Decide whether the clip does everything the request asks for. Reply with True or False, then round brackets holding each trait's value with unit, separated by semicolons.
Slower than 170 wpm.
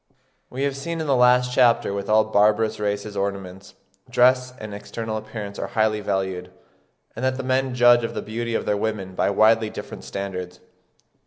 False (185 wpm)